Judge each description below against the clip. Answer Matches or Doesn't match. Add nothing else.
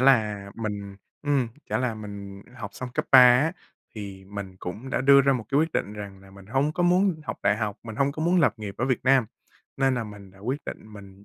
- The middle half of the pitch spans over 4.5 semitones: Matches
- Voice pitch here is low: Matches